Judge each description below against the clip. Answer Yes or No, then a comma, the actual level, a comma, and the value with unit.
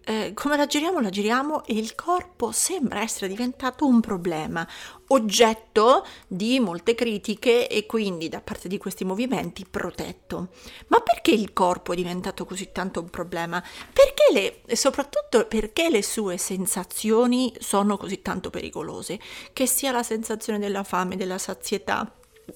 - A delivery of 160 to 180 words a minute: No, average, 150 wpm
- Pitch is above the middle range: Yes, high, 215 Hz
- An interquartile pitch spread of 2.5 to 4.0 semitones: No, average, 4.7 semitones